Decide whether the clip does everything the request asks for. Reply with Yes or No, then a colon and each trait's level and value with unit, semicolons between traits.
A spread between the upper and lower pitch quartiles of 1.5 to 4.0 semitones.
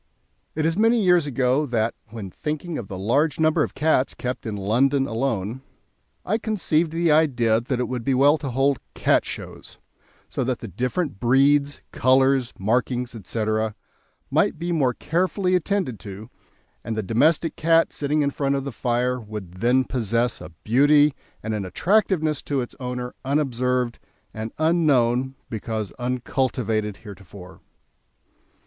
No: average, 4.8 semitones